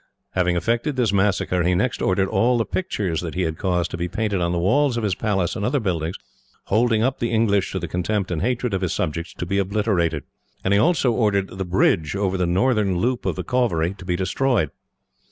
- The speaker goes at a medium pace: No, fast, 225 wpm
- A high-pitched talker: No, very low, 95 Hz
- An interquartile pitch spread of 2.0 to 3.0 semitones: No, average, 4.5 semitones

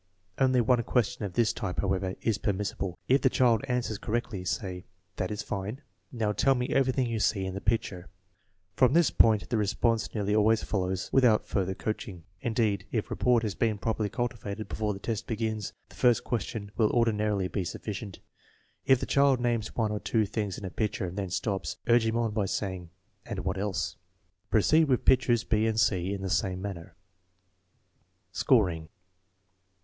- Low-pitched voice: Yes, low, 110 Hz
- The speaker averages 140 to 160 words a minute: No, average, 185 wpm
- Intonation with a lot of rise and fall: No, average, 3.3 semitones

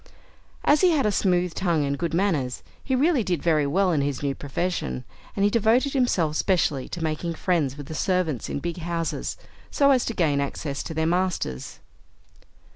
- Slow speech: No, average, 190 wpm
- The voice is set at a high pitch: No, medium, 170 Hz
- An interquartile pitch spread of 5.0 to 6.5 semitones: Yes, average, 5.3 semitones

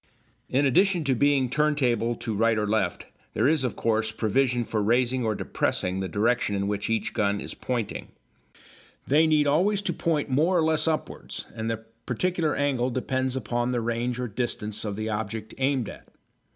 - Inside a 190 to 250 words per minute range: No, average, 180 wpm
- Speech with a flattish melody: No, average, 4.5 semitones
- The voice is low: Yes, low, 120 Hz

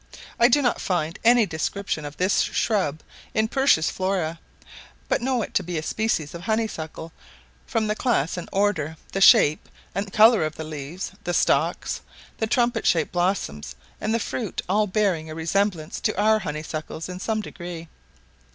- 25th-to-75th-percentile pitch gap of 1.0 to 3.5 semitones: No, average, 5.3 semitones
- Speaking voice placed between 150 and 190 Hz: Yes, medium, 185 Hz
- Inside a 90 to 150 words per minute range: No, average, 170 wpm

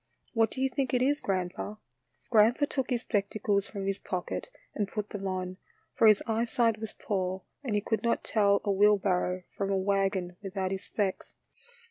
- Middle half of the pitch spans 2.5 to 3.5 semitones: Yes, average, 2.8 semitones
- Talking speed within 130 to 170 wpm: No, average, 185 wpm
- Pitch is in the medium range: No, high, 200 Hz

